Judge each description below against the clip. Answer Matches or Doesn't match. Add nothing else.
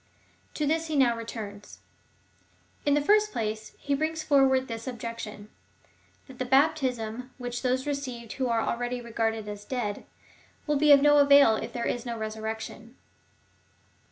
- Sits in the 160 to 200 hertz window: Doesn't match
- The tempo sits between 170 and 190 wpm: Doesn't match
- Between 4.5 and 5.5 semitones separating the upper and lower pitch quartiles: Doesn't match